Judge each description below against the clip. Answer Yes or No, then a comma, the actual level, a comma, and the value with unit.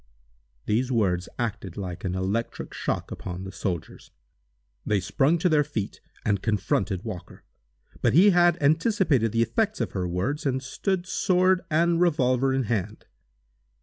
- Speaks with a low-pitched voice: Yes, low, 125 Hz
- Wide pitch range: Yes, wide, 8.9 semitones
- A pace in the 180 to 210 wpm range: No, average, 150 wpm